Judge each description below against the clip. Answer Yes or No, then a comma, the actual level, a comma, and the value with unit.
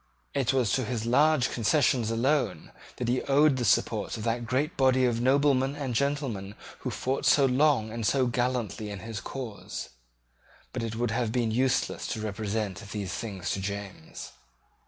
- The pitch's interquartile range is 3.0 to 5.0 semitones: Yes, average, 3.5 semitones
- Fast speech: No, average, 170 wpm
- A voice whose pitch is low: Yes, low, 120 Hz